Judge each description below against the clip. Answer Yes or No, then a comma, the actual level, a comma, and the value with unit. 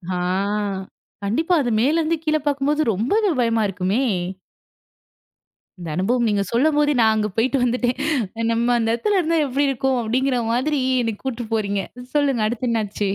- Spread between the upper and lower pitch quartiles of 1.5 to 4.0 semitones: No, average, 4.4 semitones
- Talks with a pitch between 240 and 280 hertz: Yes, high, 245 Hz